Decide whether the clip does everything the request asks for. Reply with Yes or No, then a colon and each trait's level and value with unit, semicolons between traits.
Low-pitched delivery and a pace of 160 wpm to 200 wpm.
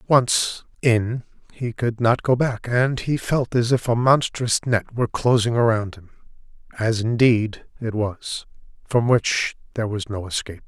Yes: low, 115 Hz; average, 165 wpm